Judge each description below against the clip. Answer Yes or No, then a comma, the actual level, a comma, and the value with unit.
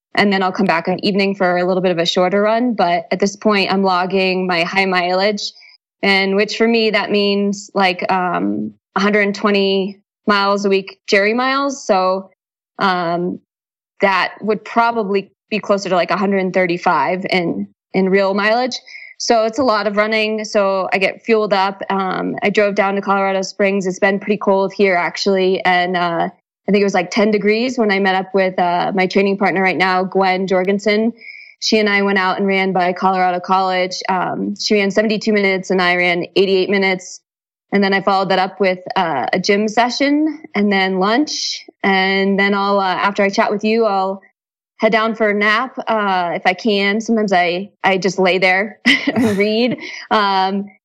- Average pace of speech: Yes, average, 190 wpm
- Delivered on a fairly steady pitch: Yes, narrow, 2.0 semitones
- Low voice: No, high, 195 Hz